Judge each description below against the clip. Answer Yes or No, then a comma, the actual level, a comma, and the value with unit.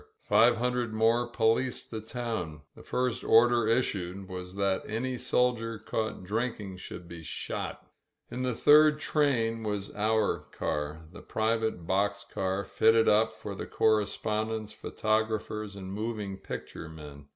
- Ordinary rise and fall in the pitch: Yes, average, 3.1 semitones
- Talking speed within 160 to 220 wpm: No, average, 140 wpm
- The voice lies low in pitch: Yes, low, 110 Hz